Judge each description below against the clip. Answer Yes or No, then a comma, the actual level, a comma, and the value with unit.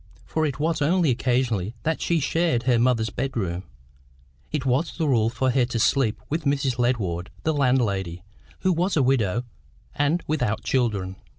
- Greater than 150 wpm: Yes, average, 165 wpm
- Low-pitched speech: Yes, low, 125 Hz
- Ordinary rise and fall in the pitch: Yes, average, 4.7 semitones